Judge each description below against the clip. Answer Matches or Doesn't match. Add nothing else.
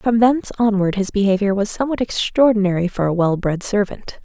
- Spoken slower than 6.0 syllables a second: Matches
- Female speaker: Matches